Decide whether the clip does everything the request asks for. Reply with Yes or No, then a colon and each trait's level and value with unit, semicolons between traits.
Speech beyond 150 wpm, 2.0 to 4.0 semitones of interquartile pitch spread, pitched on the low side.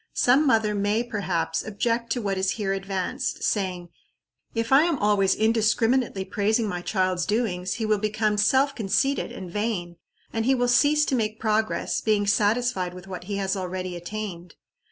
No: average, 170 wpm; average, 3.3 semitones; high, 210 Hz